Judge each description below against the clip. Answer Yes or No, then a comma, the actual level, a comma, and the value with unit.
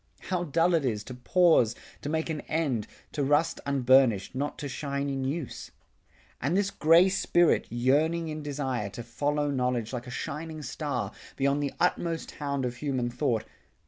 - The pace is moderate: Yes, average, 170 wpm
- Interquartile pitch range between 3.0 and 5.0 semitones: Yes, average, 4.1 semitones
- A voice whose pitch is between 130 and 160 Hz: Yes, medium, 140 Hz